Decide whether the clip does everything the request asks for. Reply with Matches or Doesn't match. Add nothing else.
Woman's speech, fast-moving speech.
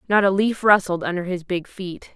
Matches